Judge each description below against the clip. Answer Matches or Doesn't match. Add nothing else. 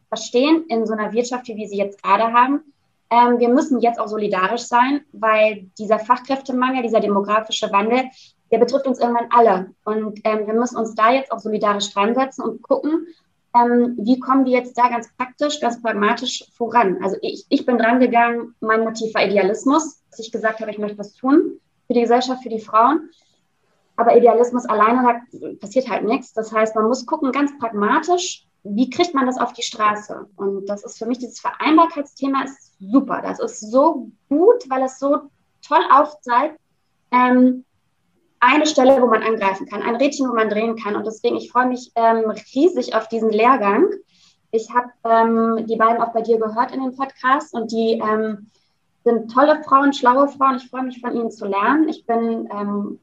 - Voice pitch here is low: Doesn't match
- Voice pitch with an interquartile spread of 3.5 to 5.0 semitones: Doesn't match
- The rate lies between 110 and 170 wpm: Doesn't match